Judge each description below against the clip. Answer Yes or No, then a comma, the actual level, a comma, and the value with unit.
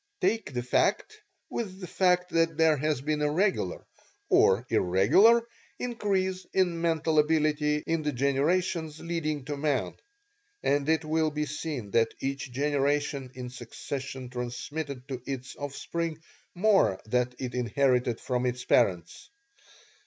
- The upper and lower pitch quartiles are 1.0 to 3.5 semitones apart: No, average, 4.6 semitones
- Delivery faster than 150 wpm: No, slow, 135 wpm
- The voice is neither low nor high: Yes, medium, 150 Hz